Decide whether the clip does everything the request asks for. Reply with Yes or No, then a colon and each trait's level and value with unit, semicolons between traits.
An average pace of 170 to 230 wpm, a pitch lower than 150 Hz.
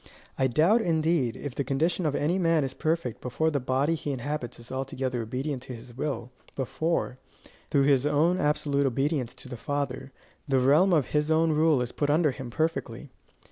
Yes: average, 185 wpm; medium, 140 Hz